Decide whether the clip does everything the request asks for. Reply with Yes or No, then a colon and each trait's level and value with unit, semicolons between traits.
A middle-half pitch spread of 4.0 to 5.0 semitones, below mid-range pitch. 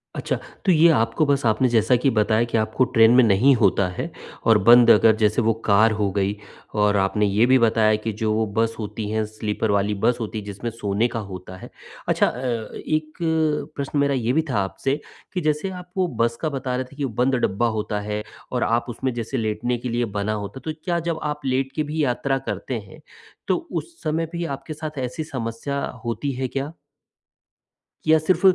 Yes: average, 4.5 semitones; low, 120 Hz